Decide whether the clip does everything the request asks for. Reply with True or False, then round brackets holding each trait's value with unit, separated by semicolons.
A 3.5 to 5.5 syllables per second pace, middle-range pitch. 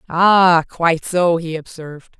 True (4.0 syllables/s; 170 Hz)